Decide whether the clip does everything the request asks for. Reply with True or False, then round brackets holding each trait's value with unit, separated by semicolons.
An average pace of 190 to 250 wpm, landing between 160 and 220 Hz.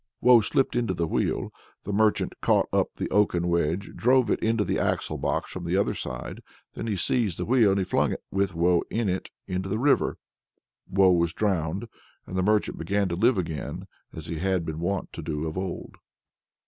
False (205 wpm; 95 Hz)